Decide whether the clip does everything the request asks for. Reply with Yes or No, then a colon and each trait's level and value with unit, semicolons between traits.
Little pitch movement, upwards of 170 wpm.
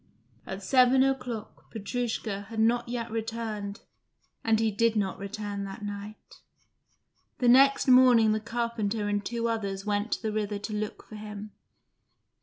No: narrow, 2.2 semitones; average, 150 wpm